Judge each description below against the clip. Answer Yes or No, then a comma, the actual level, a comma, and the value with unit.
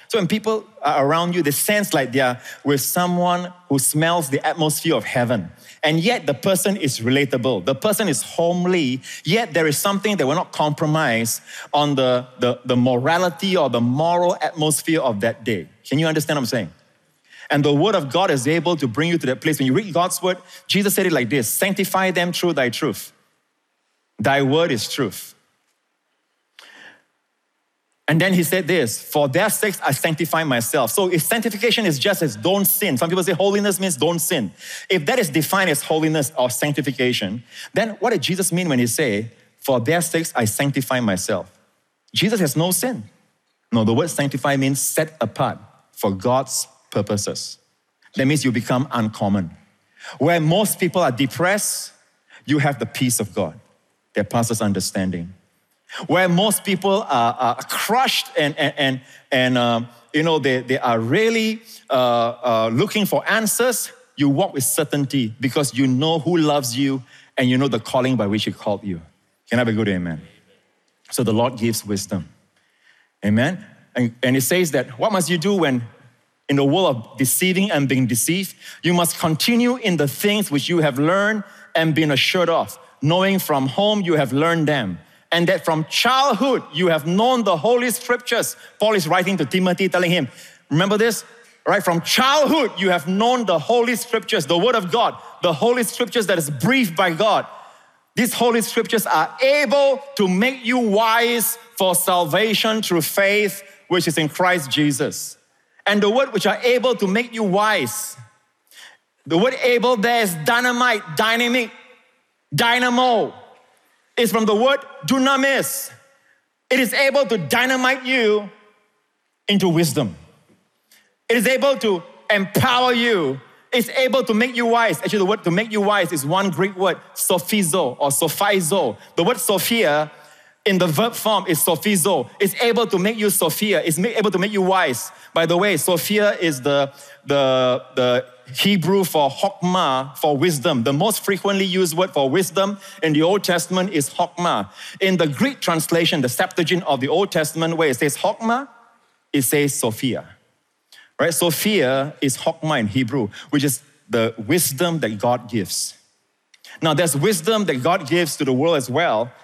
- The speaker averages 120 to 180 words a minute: Yes, average, 175 wpm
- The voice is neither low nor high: Yes, medium, 175 Hz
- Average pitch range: No, wide, 6.8 semitones